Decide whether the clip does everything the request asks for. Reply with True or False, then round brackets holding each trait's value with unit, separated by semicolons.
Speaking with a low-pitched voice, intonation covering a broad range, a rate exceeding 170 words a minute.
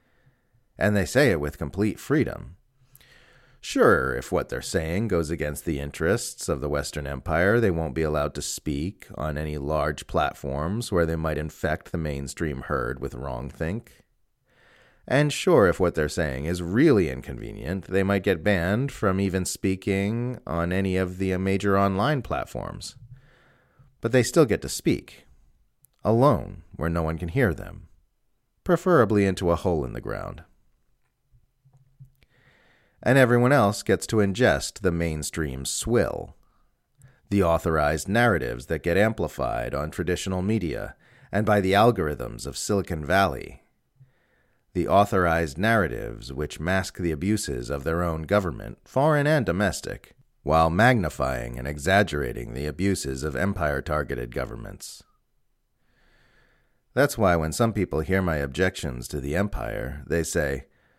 False (90 Hz; 5.9 semitones; 145 wpm)